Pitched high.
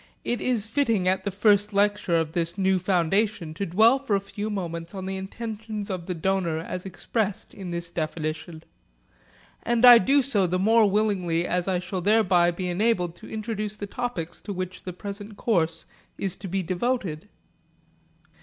Yes: high, 195 Hz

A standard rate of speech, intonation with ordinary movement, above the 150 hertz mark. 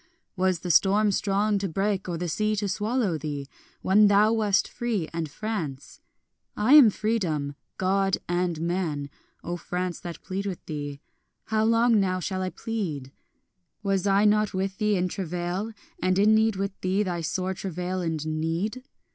Yes: average, 165 wpm; average, 3.4 semitones; high, 190 Hz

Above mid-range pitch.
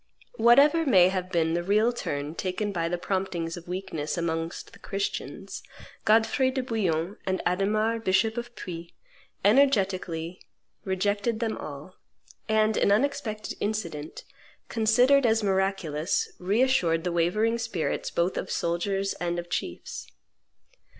Yes: high, 195 Hz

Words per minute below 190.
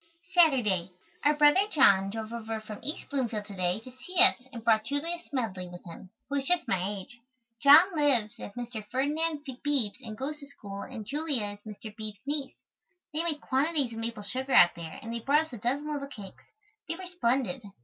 No: average, 200 wpm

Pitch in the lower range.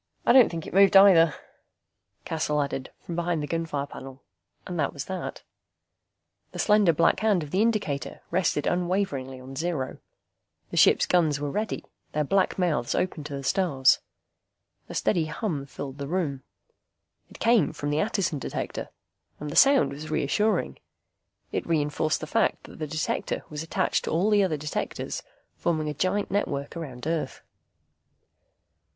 No: medium, 160 Hz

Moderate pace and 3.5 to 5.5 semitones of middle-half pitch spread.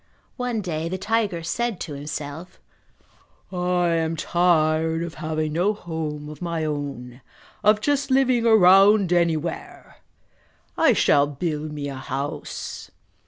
No: slow, 125 wpm; average, 4.0 semitones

